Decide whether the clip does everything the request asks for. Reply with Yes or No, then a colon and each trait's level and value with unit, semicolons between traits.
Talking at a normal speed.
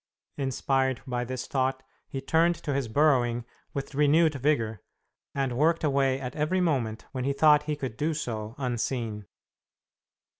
Yes: average, 150 wpm